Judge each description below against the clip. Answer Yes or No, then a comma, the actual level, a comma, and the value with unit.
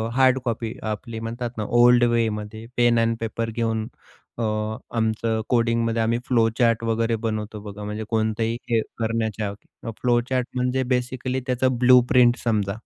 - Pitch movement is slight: Yes, narrow, 1.6 semitones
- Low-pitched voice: Yes, low, 115 Hz